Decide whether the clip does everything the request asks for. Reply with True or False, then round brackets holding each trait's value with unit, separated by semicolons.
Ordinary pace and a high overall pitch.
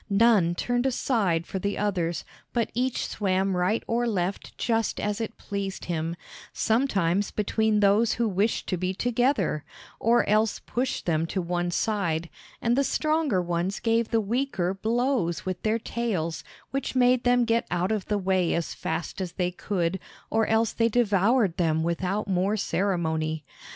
True (160 wpm; 200 Hz)